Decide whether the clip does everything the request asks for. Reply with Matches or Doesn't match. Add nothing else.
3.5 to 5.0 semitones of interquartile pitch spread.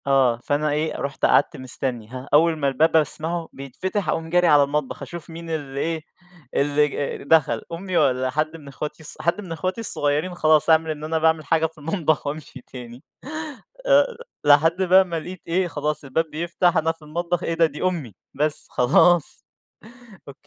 Doesn't match